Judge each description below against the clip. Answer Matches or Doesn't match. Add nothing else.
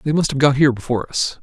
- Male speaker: Matches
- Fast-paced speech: Matches